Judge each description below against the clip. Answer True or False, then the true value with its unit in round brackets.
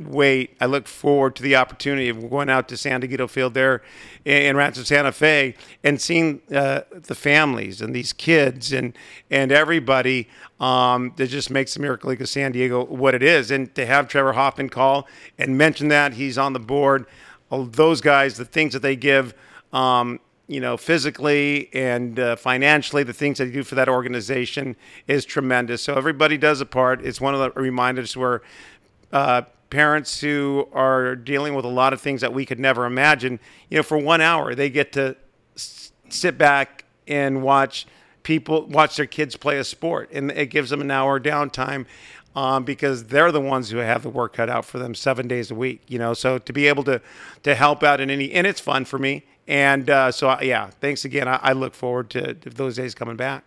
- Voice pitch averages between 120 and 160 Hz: True (135 Hz)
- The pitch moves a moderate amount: False (2.0 semitones)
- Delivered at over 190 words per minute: True (205 wpm)